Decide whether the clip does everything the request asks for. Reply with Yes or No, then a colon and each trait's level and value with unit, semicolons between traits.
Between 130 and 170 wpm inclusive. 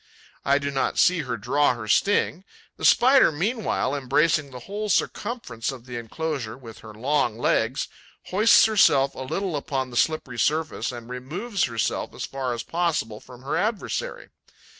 Yes: average, 160 wpm